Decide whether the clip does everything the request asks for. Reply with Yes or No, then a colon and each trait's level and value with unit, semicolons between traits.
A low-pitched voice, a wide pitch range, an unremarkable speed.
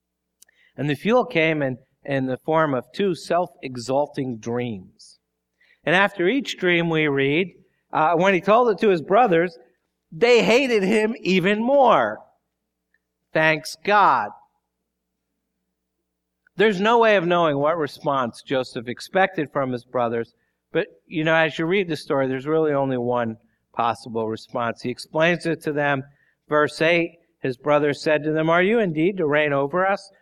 No: medium, 155 Hz; wide, 6.1 semitones; average, 155 wpm